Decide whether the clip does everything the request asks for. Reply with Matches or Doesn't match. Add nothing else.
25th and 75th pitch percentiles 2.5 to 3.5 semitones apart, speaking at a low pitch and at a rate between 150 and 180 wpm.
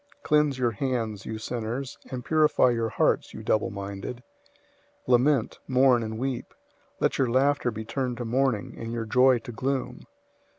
Matches